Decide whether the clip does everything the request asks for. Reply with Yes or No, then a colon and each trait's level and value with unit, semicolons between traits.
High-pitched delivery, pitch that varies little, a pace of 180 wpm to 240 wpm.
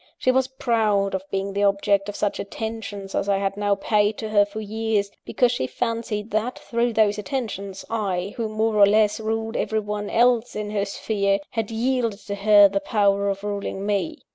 Yes: high, 210 Hz; narrow, 2.0 semitones; average, 190 wpm